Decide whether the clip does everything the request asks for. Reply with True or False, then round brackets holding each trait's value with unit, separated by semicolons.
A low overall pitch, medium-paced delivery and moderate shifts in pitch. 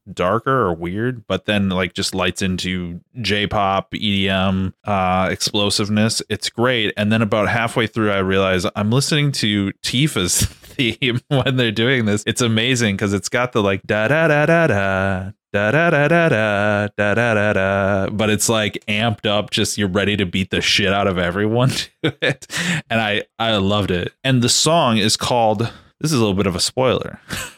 True (105 Hz; 185 wpm; 3.2 semitones)